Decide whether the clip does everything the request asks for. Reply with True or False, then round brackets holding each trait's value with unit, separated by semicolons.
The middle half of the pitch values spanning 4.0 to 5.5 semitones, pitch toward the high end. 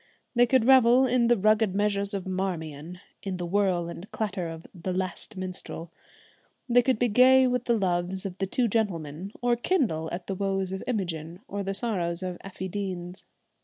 True (4.3 semitones; 195 Hz)